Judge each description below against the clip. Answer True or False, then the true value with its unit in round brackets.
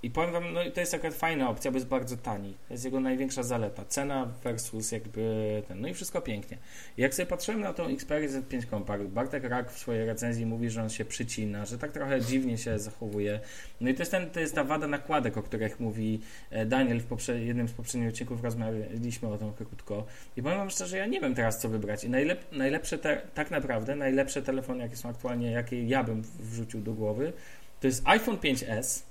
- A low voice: True (120 Hz)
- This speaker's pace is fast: True (220 wpm)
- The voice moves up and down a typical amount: True (3.4 semitones)